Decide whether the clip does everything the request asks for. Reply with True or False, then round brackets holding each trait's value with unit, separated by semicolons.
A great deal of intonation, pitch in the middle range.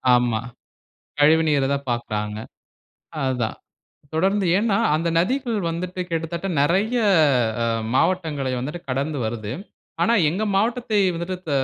True (6.6 semitones; 165 Hz)